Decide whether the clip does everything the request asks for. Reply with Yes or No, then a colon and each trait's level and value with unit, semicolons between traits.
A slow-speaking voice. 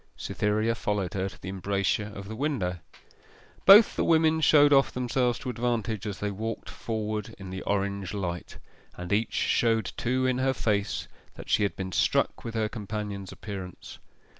No: average, 170 wpm